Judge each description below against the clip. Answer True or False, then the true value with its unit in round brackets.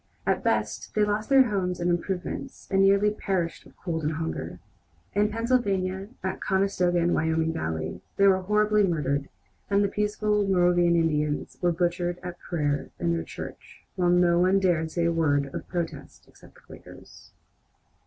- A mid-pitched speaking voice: True (180 Hz)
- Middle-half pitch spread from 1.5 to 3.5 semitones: True (3.1 semitones)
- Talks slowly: False (165 wpm)